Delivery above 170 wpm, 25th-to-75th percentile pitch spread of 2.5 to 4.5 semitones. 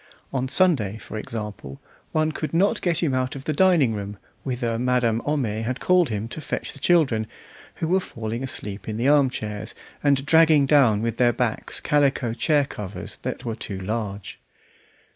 No: average, 180 wpm; average, 5.3 semitones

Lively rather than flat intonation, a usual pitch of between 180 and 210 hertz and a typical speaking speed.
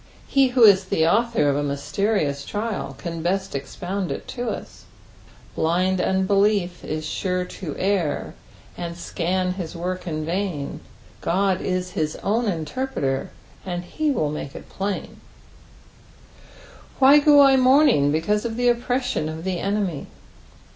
No: average, 4.8 semitones; medium, 185 Hz; average, 145 wpm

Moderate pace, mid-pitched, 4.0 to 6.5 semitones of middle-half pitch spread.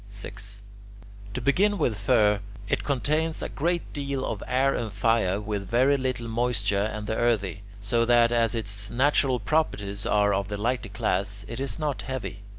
No: average, 170 wpm; low, 115 Hz; average, 4.4 semitones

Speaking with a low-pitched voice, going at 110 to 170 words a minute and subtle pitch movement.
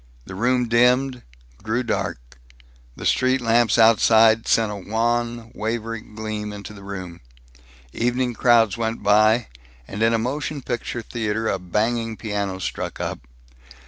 Yes: low, 115 Hz; average, 140 wpm; narrow, 2.1 semitones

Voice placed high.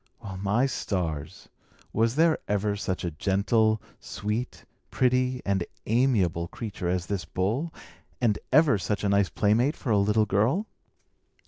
No: low, 105 Hz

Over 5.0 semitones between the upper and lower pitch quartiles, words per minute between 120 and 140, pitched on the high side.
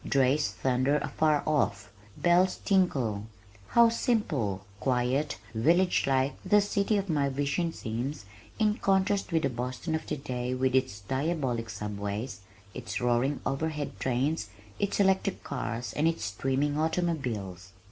No: wide, 5.5 semitones; slow, 135 wpm; medium, 140 Hz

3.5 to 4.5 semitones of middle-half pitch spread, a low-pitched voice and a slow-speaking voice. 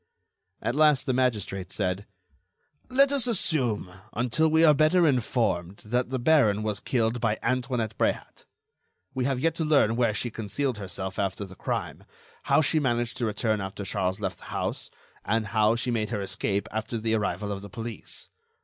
No: average, 4.2 semitones; low, 115 Hz; average, 175 wpm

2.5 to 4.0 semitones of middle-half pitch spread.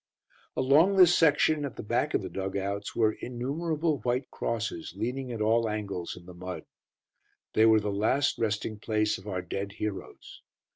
No: average, 5.1 semitones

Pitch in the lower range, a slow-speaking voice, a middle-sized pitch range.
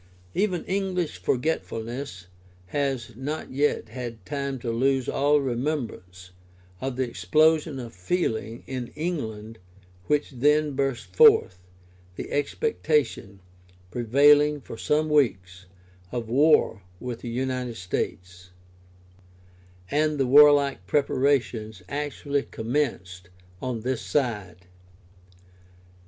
Yes: low, 130 Hz; slow, 100 wpm; average, 4.7 semitones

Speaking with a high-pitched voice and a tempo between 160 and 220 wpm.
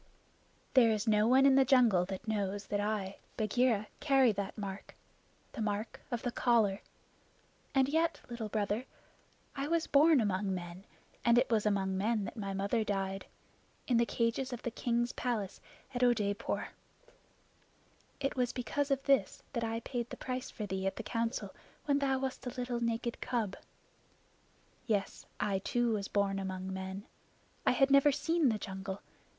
Yes: high, 225 Hz; average, 165 wpm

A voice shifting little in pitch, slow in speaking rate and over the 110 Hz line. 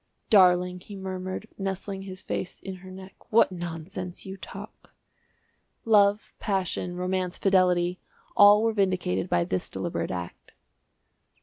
Yes: narrow, 1.4 semitones; slow, 125 wpm; medium, 185 Hz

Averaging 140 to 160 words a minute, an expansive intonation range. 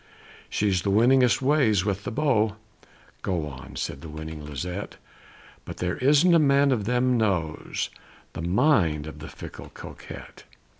Yes: average, 150 wpm; wide, 7.9 semitones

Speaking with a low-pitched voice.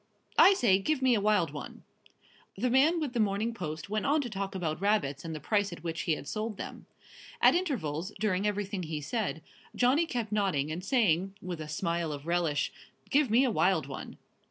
No: high, 195 Hz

